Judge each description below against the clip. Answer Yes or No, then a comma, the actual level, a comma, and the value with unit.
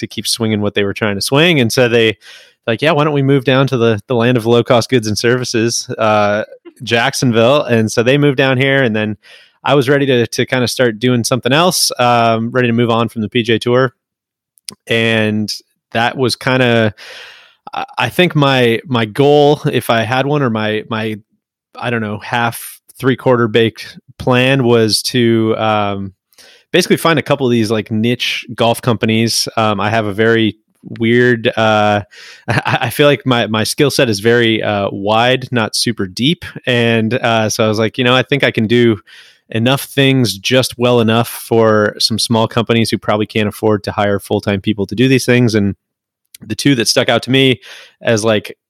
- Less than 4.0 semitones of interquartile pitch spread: Yes, average, 2.7 semitones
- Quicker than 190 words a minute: Yes, average, 200 wpm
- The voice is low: Yes, low, 115 Hz